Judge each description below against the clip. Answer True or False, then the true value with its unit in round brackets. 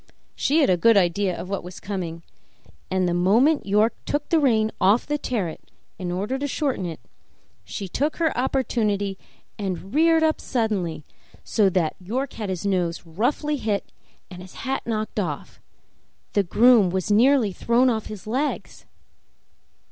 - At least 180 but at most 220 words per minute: False (160 wpm)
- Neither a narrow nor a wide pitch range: False (5.7 semitones)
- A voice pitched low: False (210 Hz)